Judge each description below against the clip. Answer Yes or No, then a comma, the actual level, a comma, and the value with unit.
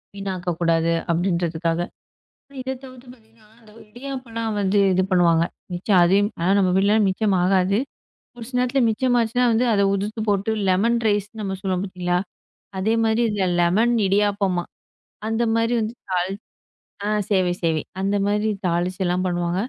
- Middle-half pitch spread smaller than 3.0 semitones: No, average, 3.7 semitones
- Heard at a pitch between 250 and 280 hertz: No, high, 200 Hz